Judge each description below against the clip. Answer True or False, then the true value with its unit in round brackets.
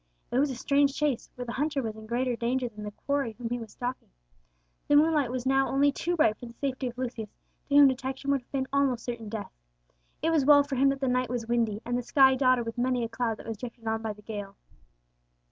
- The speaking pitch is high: True (250 Hz)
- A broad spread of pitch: False (3.0 semitones)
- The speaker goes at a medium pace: False (250 wpm)